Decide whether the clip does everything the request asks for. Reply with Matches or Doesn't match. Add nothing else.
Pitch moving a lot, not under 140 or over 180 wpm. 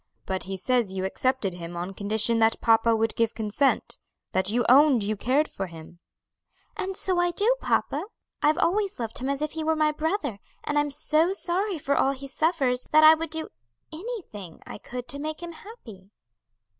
Doesn't match